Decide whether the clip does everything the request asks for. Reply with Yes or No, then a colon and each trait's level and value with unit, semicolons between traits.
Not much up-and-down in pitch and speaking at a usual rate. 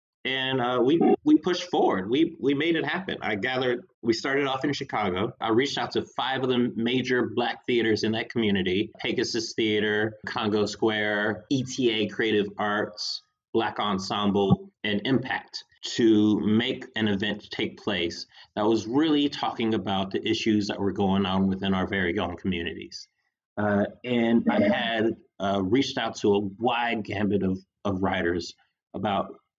No: average, 3.8 semitones; average, 160 wpm